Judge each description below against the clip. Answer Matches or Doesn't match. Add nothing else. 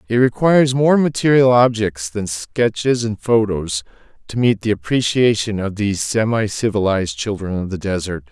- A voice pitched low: Matches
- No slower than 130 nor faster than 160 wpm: Matches